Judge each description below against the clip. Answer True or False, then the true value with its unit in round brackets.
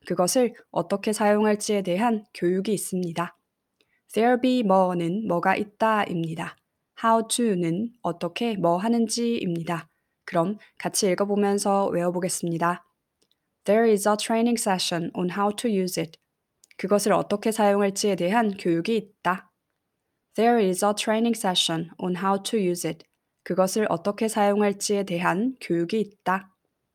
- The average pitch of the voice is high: True (200 Hz)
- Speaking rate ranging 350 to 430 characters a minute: True (385 characters per minute)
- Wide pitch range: False (3.6 semitones)